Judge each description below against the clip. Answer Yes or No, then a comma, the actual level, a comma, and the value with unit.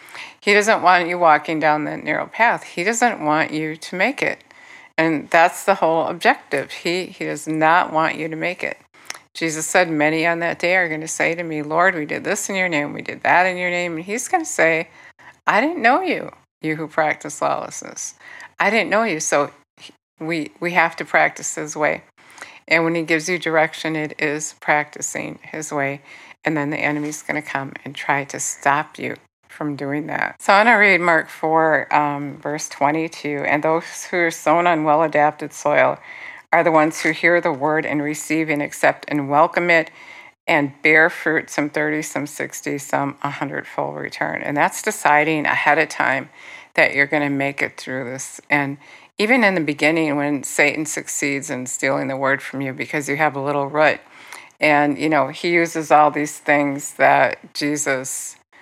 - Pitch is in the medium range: Yes, medium, 155 Hz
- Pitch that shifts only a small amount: Yes, narrow, 2.2 semitones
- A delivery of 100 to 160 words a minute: No, average, 195 wpm